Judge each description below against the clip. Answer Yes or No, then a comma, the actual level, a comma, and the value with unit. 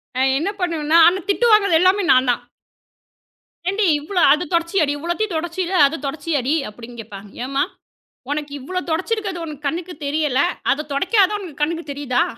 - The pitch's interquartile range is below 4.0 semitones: No, average, 4.5 semitones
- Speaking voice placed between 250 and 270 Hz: No, very high, 320 Hz